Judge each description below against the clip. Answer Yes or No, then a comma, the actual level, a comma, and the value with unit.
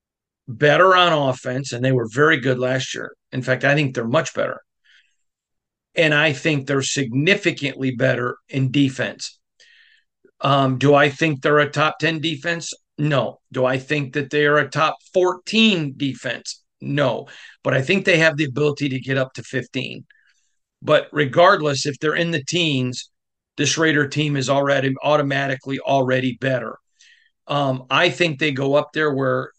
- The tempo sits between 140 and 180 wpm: Yes, average, 165 wpm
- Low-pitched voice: No, medium, 145 Hz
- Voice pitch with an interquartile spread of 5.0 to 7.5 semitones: No, average, 2.8 semitones